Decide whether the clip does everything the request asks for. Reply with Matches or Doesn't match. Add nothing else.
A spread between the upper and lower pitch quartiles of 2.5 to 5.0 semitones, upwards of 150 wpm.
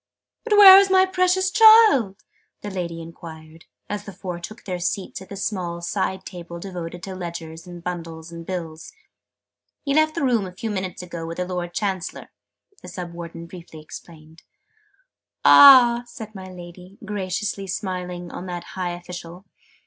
Matches